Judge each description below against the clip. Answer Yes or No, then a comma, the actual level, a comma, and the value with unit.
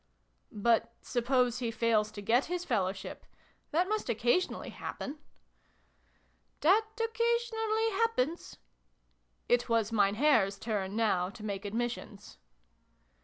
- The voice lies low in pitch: No, high, 235 Hz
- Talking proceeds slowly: Yes, slow, 120 wpm